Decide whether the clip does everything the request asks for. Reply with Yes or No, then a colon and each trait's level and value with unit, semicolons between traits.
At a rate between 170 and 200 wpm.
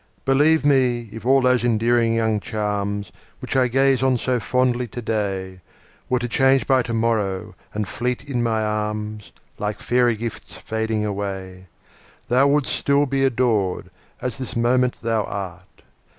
No: average, 150 wpm